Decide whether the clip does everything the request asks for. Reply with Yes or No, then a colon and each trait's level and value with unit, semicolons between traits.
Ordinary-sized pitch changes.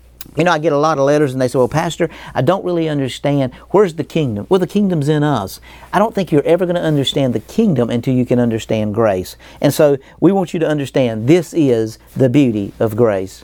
No: wide, 5.7 semitones